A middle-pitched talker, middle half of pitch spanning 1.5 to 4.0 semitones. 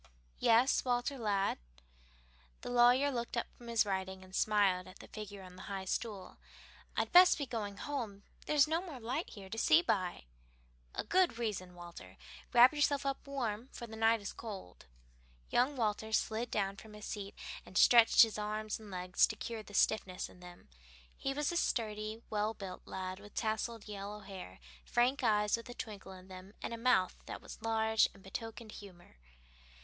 No: high, 215 Hz; average, 3.5 semitones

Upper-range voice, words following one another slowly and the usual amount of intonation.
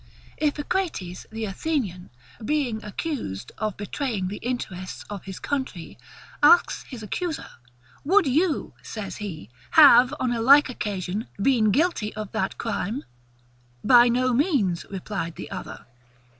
No: high, 225 Hz; slow, 130 wpm; wide, 6.1 semitones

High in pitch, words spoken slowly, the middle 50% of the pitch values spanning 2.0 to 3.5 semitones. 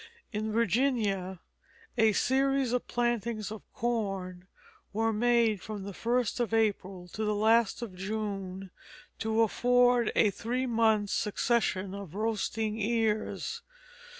Yes: high, 220 Hz; slow, 125 wpm; average, 2.9 semitones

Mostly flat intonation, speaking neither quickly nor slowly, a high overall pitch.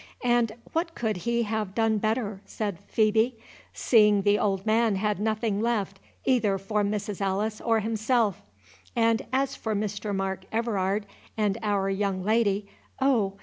Yes: narrow, 2.2 semitones; average, 145 wpm; high, 215 Hz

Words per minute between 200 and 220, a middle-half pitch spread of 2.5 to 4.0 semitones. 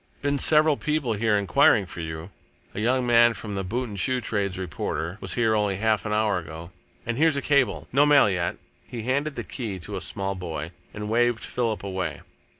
No: fast, 205 wpm; average, 4.6 semitones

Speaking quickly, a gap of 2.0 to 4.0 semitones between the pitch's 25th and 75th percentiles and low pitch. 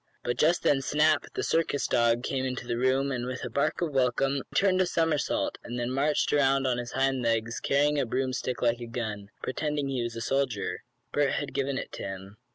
Yes: fast, 220 wpm; average, 2.9 semitones; low, 130 Hz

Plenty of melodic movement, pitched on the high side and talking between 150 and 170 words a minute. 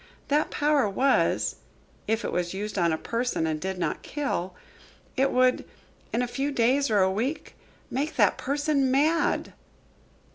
Yes: wide, 6.6 semitones; very high, 250 Hz; average, 155 wpm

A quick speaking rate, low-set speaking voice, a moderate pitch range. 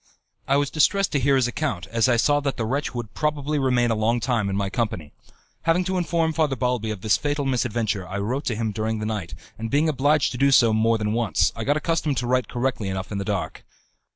Yes: fast, 240 wpm; low, 120 Hz; average, 4.7 semitones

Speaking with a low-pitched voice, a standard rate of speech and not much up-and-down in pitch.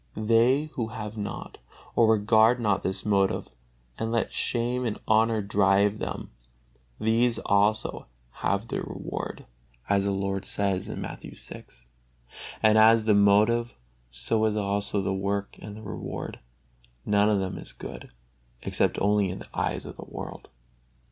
Yes: low, 105 Hz; average, 150 wpm; narrow, 2.1 semitones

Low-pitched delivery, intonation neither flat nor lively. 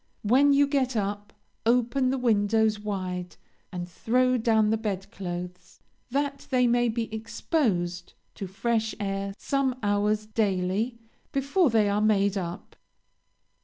No: high, 220 Hz; average, 4.0 semitones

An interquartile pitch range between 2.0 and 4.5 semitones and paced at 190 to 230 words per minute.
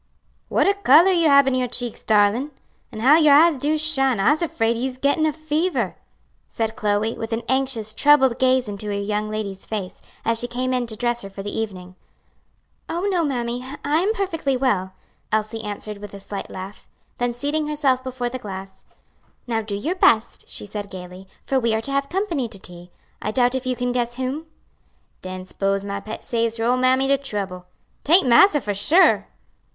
No: average, 5.0 semitones; average, 200 wpm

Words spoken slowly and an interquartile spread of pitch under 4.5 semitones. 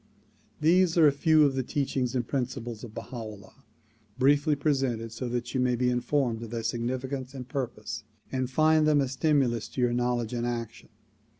No: average, 185 wpm; average, 2.9 semitones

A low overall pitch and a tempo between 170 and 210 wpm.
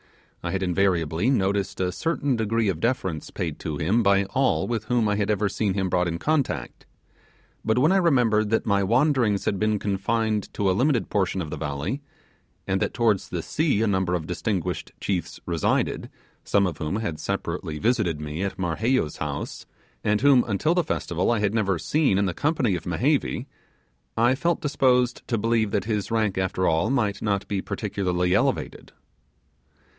Yes: low, 100 Hz; average, 180 wpm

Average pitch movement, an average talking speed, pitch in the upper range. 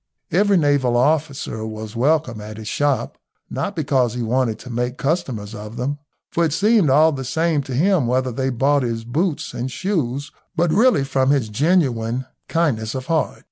No: average, 4.7 semitones; average, 180 wpm; low, 135 Hz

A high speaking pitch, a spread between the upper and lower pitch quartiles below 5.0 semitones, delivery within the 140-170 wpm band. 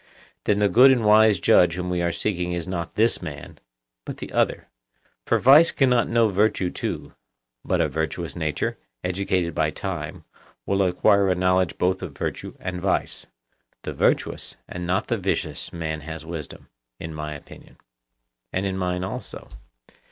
No: very low, 90 Hz; average, 3.3 semitones; average, 160 wpm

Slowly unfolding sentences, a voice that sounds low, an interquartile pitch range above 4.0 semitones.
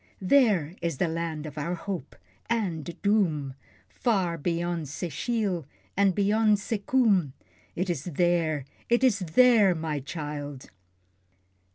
No: slow, 120 wpm; medium, 175 Hz; average, 4.7 semitones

